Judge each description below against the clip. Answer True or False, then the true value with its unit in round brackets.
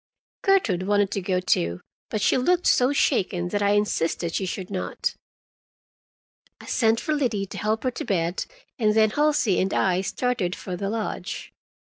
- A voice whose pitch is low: False (205 Hz)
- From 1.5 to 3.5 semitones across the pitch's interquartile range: False (4.3 semitones)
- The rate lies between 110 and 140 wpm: False (170 wpm)